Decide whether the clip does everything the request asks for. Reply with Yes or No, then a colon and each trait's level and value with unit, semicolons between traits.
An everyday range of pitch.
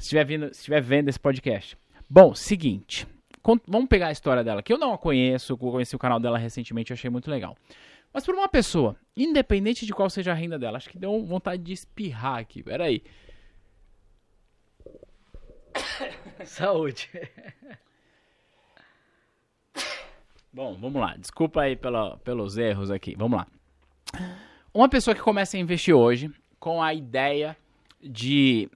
No: wide, 8.0 semitones